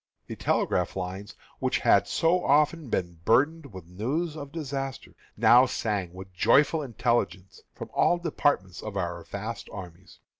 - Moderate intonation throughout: No, wide, 7.7 semitones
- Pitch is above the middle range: No, low, 115 Hz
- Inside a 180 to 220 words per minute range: No, average, 145 wpm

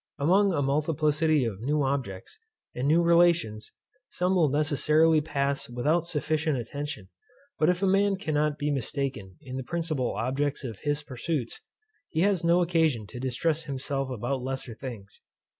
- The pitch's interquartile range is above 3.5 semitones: Yes, average, 3.9 semitones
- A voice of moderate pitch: Yes, medium, 145 Hz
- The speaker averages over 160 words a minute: No, average, 155 wpm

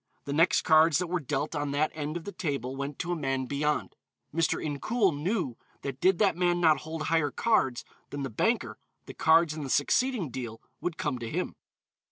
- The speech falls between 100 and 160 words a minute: No, fast, 205 wpm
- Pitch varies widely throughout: No, average, 3.6 semitones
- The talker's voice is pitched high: No, medium, 155 Hz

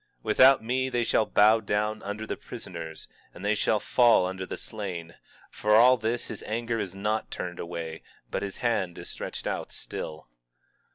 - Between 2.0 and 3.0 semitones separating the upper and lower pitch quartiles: No, average, 3.5 semitones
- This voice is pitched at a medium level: No, low, 105 Hz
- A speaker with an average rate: Yes, average, 180 wpm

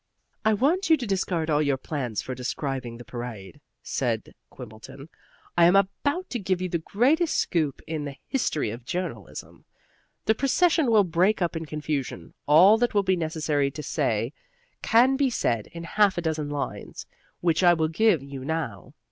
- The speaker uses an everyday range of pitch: No, wide, 6.9 semitones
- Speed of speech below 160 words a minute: No, average, 175 wpm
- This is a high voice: No, medium, 165 Hz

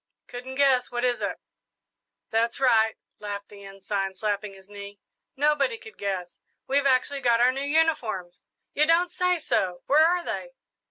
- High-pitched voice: Yes, high, 245 Hz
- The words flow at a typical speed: Yes, average, 160 wpm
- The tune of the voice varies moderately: No, wide, 6.3 semitones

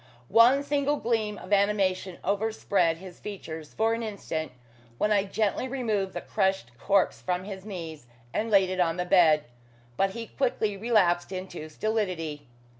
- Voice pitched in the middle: No, high, 195 Hz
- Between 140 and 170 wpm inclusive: Yes, average, 155 wpm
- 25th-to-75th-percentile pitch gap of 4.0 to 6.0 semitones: No, average, 3.5 semitones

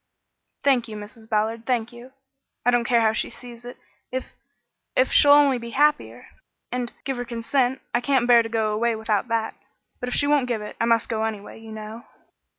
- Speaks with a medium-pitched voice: No, high, 235 Hz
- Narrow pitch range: Yes, narrow, 2.1 semitones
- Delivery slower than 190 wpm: No, fast, 205 wpm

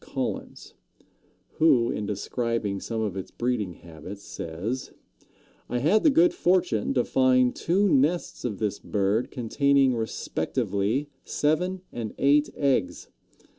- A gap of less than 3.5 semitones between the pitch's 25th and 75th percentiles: No, wide, 5.6 semitones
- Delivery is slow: Yes, slow, 125 wpm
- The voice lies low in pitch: Yes, low, 125 Hz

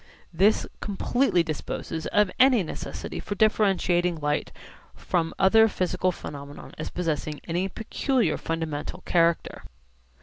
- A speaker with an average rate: No, slow, 110 wpm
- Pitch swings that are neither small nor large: Yes, average, 4.2 semitones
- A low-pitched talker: No, medium, 180 Hz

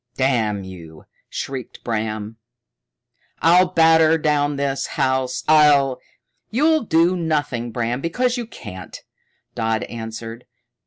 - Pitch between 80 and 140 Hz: Yes, low, 135 Hz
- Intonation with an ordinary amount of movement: No, wide, 6.2 semitones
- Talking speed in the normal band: No, slow, 110 wpm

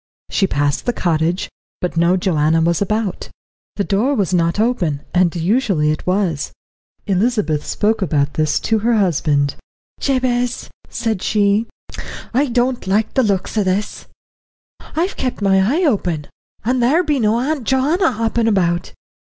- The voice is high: Yes, high, 200 Hz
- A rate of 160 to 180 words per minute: No, average, 150 wpm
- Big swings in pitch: Yes, wide, 5.9 semitones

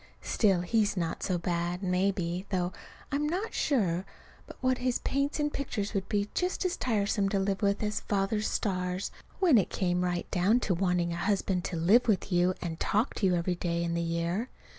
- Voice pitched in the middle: No, high, 195 Hz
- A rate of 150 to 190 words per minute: No, average, 200 wpm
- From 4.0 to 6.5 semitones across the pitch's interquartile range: No, average, 3.6 semitones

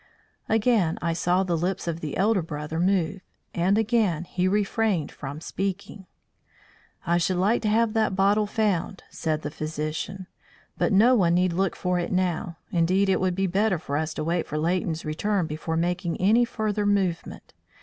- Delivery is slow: No, average, 175 wpm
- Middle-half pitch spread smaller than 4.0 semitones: Yes, average, 3.4 semitones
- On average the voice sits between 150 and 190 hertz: Yes, medium, 185 Hz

